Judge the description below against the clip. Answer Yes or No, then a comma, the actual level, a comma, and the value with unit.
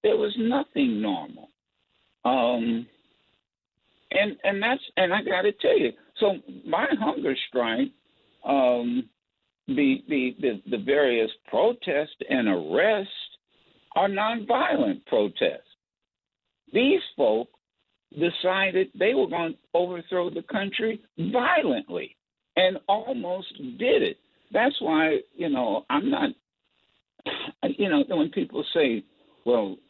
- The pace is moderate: No, slow, 110 wpm